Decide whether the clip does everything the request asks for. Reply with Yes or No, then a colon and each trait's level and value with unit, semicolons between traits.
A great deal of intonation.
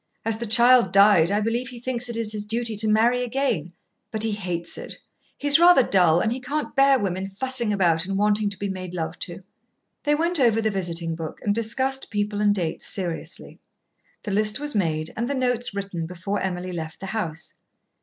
No: average, 4.6 semitones